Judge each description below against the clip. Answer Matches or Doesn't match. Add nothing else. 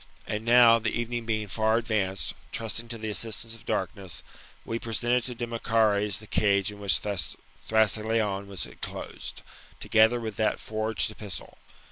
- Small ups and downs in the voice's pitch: Matches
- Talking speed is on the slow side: Doesn't match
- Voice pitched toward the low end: Matches